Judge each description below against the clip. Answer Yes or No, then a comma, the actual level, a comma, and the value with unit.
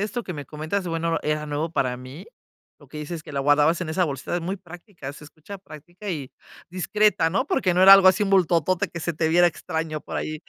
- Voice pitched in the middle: Yes, medium, 165 Hz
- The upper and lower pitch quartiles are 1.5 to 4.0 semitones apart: Yes, average, 3.4 semitones